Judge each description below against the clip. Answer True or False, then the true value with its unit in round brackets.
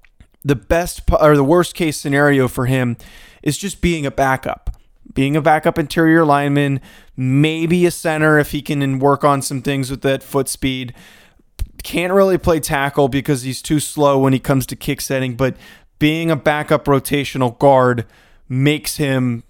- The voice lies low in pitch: False (145 Hz)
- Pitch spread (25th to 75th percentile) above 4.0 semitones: False (2.5 semitones)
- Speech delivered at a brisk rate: False (170 wpm)